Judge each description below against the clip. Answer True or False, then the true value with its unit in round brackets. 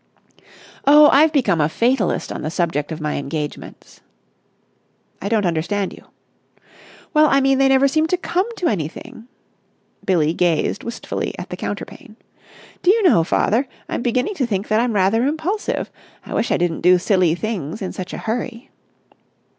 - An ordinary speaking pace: True (165 wpm)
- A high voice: True (220 Hz)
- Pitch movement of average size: False (7.7 semitones)